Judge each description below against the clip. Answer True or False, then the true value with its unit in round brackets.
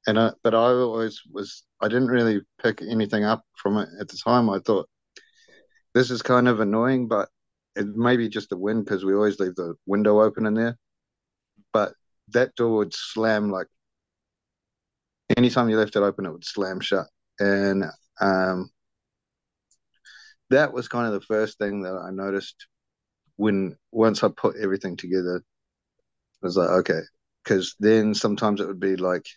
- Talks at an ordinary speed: True (170 wpm)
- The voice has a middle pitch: False (110 Hz)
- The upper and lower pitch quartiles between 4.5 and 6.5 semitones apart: False (2.8 semitones)